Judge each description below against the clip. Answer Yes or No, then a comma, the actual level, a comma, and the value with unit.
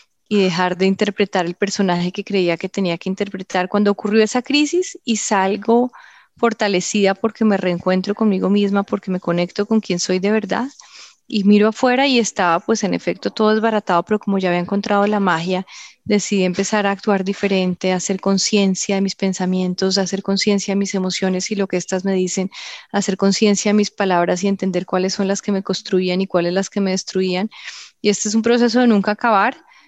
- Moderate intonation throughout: No, narrow, 2.1 semitones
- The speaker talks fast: Yes, fast, 200 wpm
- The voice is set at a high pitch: Yes, high, 195 Hz